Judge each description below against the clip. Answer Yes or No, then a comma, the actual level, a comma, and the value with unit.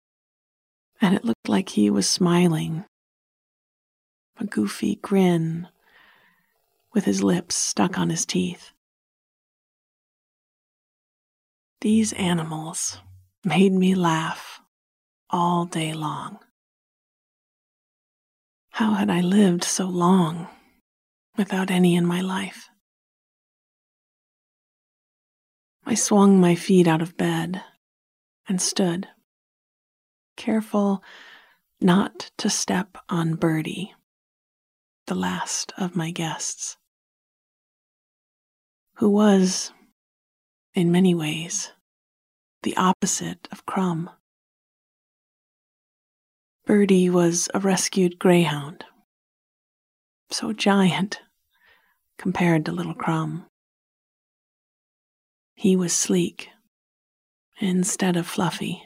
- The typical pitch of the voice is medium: Yes, medium, 180 Hz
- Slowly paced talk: Yes, slow, 85 wpm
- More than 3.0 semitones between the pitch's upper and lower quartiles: No, narrow, 2.6 semitones